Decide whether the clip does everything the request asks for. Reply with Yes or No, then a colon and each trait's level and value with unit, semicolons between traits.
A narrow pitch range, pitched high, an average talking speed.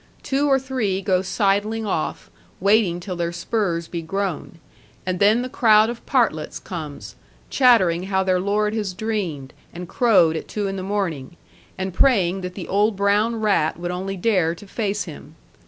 No: average, 3.5 semitones; high, 195 Hz; average, 170 wpm